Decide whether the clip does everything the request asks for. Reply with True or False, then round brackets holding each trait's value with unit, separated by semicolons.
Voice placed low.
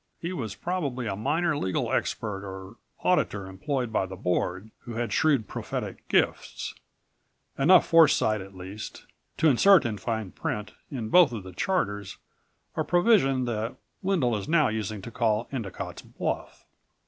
True (115 Hz)